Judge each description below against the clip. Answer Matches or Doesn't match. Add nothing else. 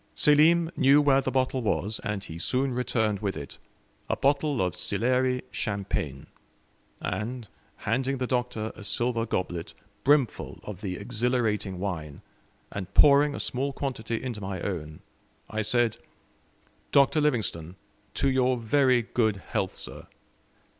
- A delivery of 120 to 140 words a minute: Matches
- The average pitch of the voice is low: Matches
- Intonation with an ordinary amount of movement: Matches